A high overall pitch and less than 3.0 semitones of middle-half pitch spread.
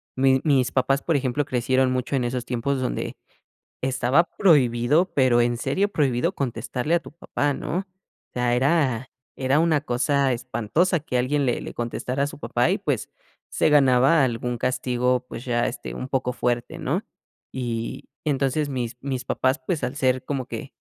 No: low, 130 Hz; narrow, 2.6 semitones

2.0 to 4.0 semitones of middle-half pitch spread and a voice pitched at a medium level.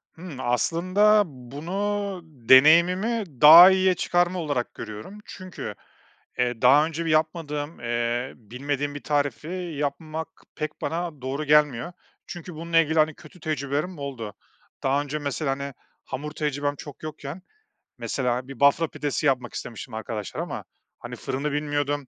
Yes: average, 3.6 semitones; medium, 145 Hz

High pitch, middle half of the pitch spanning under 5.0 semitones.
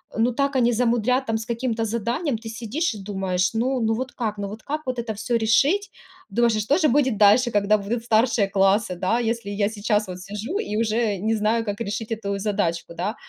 Yes: high, 225 Hz; average, 2.8 semitones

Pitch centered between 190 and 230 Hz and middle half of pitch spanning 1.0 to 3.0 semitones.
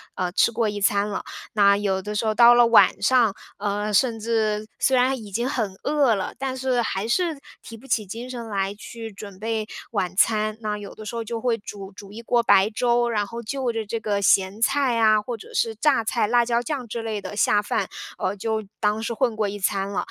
Yes: high, 220 Hz; narrow, 2.5 semitones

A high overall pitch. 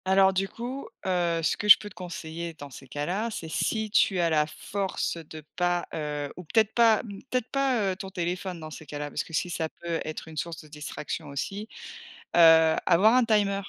No: medium, 175 Hz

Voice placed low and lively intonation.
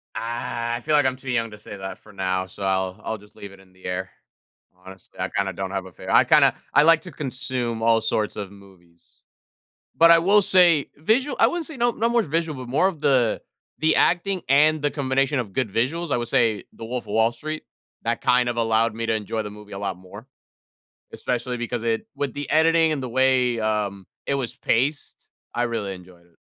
Yes: low, 120 Hz; wide, 6.2 semitones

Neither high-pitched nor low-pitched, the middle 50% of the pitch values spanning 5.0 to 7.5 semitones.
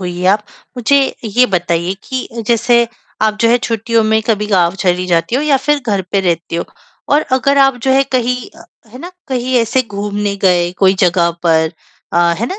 No: high, 215 Hz; wide, 5.5 semitones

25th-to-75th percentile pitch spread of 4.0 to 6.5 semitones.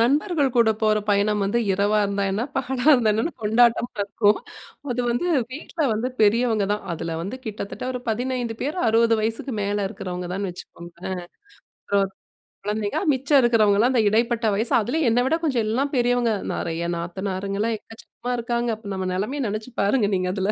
No: average, 3.5 semitones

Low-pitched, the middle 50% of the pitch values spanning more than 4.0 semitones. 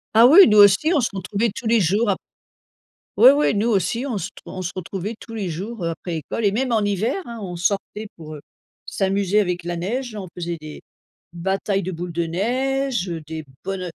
No: high, 200 Hz; average, 4.5 semitones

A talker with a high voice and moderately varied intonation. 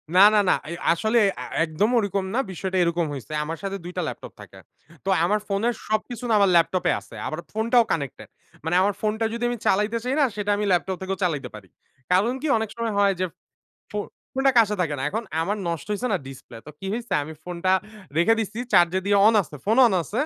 Yes: high, 195 Hz; average, 4.4 semitones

